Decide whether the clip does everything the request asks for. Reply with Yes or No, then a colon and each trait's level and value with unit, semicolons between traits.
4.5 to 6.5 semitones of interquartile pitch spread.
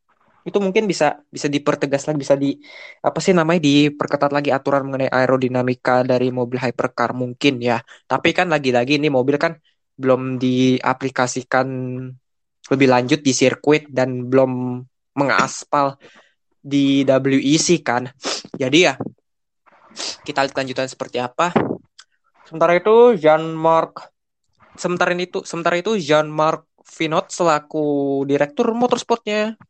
No: average, 4.1 semitones